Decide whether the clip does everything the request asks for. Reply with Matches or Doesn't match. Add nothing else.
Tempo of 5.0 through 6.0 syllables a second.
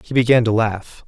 Matches